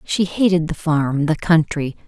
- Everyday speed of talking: Yes, average, 175 wpm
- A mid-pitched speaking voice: Yes, medium, 160 Hz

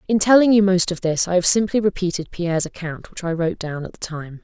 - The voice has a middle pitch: Yes, medium, 180 Hz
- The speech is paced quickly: Yes, fast, 255 wpm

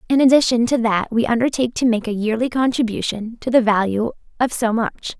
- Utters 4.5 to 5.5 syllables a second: No, 5.7 syllables/s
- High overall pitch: Yes, high, 230 Hz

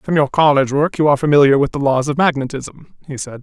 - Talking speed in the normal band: No, fast, 245 wpm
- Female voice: No, male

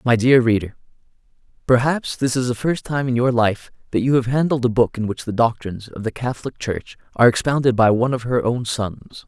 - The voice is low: Yes, low, 120 Hz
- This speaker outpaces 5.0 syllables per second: Yes, 5.7 syllables/s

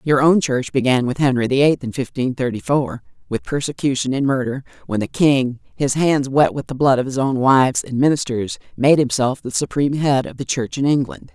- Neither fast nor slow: No, fast, 215 wpm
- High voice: No, low, 135 Hz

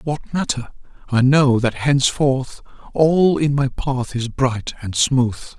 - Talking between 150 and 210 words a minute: No, average, 140 wpm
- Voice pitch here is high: No, low, 130 Hz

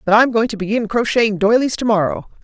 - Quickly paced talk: No, average, 195 wpm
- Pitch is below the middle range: No, high, 220 Hz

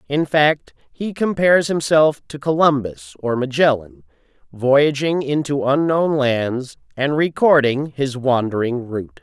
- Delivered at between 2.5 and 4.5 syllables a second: Yes, 4.0 syllables/s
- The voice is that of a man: Yes, male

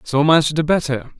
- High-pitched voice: No, medium, 150 Hz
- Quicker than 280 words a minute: No, average, 200 wpm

